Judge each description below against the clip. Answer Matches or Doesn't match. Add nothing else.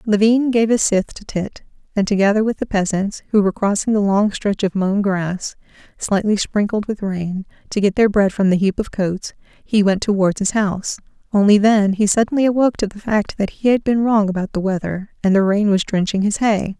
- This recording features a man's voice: Doesn't match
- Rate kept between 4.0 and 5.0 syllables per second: Doesn't match